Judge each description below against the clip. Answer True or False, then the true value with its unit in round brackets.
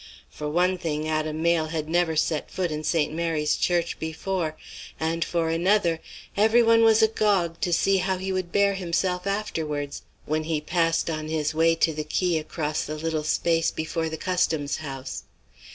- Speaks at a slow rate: False (175 wpm)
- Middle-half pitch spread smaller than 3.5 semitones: True (2.7 semitones)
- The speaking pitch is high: False (165 Hz)